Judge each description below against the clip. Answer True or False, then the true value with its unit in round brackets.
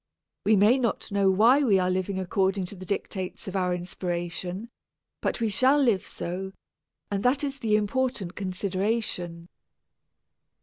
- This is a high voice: True (195 Hz)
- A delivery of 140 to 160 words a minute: True (145 wpm)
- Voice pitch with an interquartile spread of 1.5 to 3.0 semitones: False (3.6 semitones)